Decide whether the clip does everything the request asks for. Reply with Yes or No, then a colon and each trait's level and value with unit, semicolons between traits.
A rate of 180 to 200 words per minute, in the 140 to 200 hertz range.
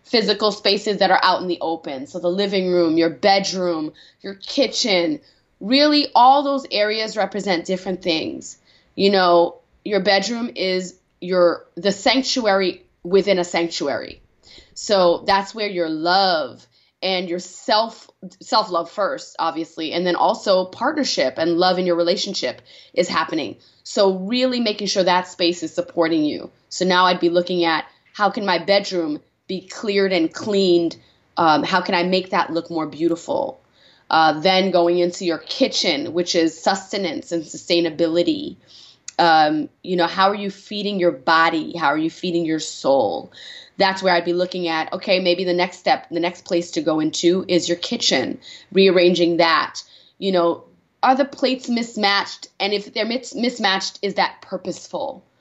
No: average, 160 wpm; medium, 185 Hz